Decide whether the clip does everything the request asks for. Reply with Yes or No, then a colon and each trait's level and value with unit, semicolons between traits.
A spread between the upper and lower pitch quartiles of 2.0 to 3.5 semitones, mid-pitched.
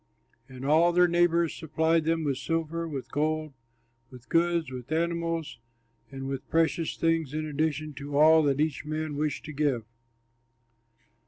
Yes: narrow, 2.5 semitones; medium, 155 Hz